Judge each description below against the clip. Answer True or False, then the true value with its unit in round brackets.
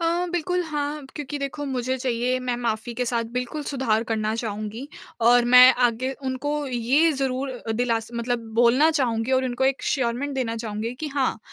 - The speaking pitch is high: True (255 Hz)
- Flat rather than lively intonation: False (3.2 semitones)